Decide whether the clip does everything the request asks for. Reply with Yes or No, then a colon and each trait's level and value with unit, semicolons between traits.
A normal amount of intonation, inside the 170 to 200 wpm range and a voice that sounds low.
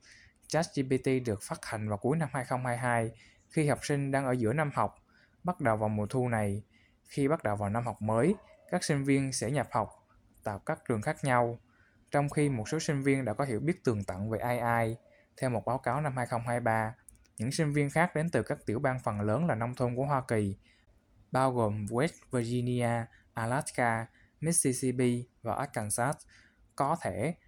Yes: average, 4.1 semitones; average, 190 wpm; low, 120 Hz